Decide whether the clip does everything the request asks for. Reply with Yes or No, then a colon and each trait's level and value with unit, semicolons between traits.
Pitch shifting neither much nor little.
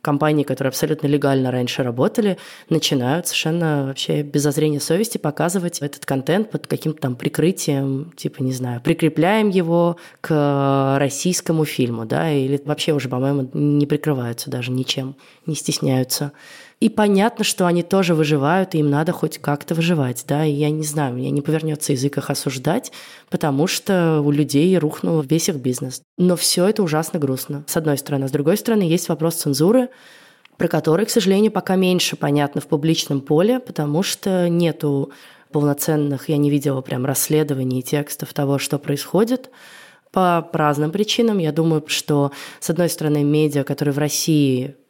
Yes: average, 3.3 semitones